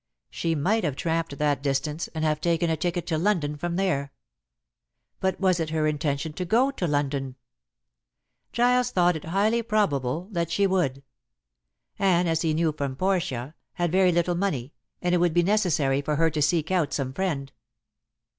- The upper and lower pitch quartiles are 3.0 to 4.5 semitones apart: Yes, average, 3.9 semitones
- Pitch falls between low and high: Yes, medium, 165 Hz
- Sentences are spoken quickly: No, average, 175 wpm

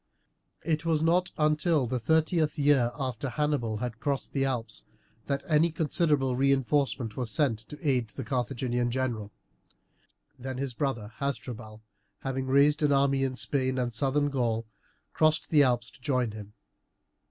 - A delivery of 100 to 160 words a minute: Yes, average, 150 wpm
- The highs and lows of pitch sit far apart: No, average, 3.4 semitones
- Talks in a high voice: No, low, 135 Hz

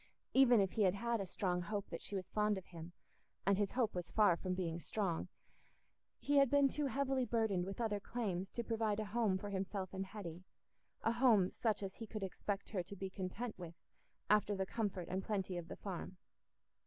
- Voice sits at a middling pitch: No, high, 200 Hz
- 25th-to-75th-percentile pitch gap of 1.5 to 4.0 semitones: Yes, average, 3.3 semitones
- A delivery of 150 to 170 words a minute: No, average, 200 wpm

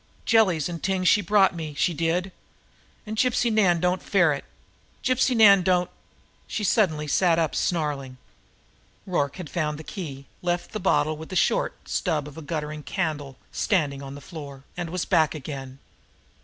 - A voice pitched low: No, medium, 165 Hz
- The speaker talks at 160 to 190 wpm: Yes, average, 165 wpm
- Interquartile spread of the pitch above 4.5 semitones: No, average, 4.1 semitones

